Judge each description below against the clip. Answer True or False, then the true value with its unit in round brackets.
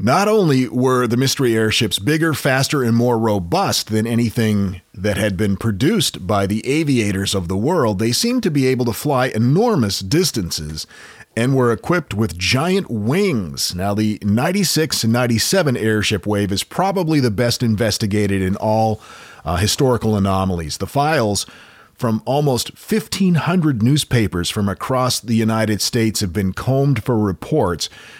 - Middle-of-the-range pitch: False (115 Hz)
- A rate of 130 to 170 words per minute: True (150 wpm)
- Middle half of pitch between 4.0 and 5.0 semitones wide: True (4.3 semitones)